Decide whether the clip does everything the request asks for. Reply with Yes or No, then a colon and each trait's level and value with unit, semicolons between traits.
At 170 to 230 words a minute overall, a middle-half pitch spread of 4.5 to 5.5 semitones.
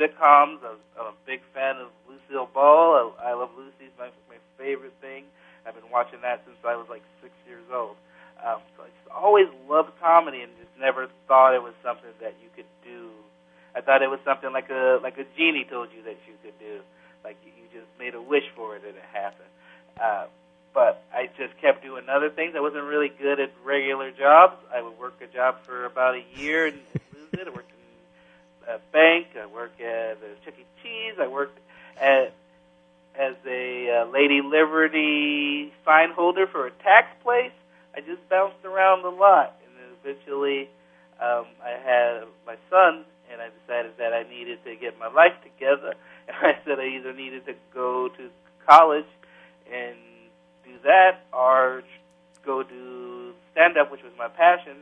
Yes: average, 195 wpm; average, 4.8 semitones